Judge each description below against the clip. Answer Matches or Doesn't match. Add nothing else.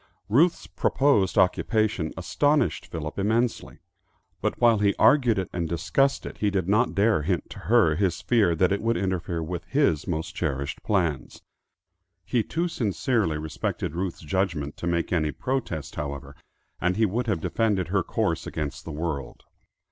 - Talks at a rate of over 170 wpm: Doesn't match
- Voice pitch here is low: Matches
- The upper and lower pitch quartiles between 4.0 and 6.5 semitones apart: Matches